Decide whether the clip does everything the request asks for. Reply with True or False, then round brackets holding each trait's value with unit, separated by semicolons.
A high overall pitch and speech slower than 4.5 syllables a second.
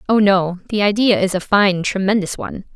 False (200 Hz; 5.4 syllables/s)